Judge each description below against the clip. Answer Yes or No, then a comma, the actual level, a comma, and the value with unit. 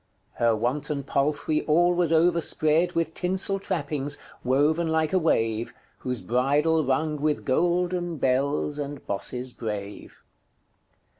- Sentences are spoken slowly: Yes, slow, 120 wpm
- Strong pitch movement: No, average, 4.1 semitones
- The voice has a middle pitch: Yes, medium, 150 Hz